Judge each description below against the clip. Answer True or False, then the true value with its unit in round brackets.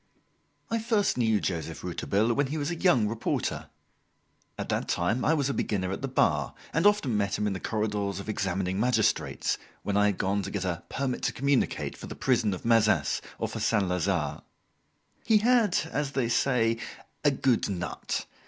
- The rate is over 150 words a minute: True (190 wpm)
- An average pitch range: False (5.9 semitones)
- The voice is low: True (110 Hz)